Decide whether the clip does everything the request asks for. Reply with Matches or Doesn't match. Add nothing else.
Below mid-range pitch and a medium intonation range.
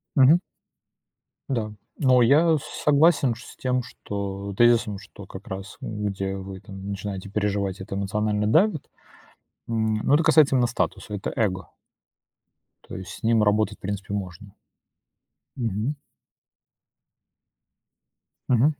Matches